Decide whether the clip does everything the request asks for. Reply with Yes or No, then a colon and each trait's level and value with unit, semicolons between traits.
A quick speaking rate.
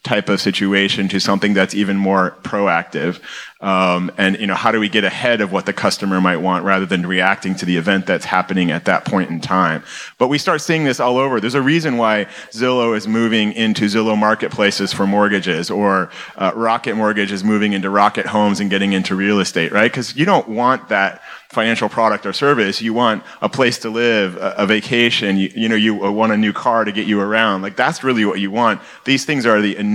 Yes: fast, 220 wpm